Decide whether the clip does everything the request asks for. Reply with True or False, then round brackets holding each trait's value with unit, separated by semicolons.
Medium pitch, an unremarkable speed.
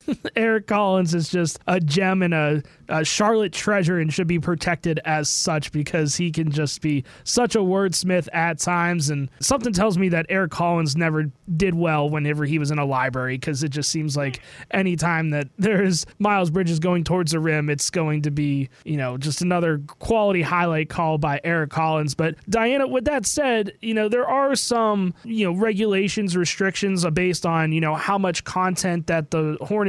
True (170 Hz; 190 wpm)